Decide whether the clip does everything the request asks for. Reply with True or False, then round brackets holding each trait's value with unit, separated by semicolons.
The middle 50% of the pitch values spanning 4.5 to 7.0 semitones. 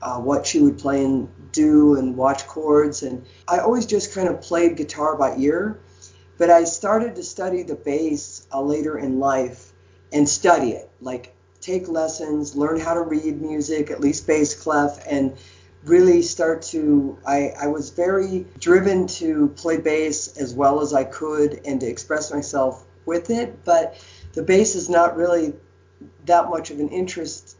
False (3.8 semitones)